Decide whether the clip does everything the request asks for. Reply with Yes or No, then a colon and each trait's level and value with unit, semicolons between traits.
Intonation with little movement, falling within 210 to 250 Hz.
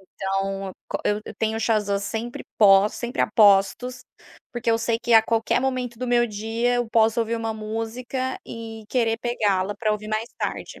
Yes: narrow, 2.1 semitones; high, 225 Hz